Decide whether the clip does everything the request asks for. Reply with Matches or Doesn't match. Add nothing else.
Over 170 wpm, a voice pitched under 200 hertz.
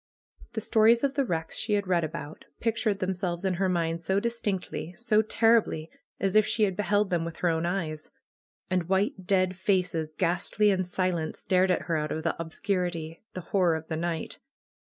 Matches